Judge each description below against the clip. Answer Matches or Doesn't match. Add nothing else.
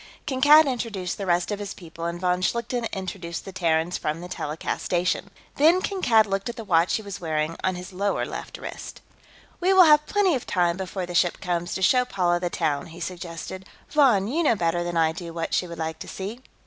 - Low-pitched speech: Doesn't match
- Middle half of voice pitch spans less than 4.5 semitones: Doesn't match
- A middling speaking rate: Doesn't match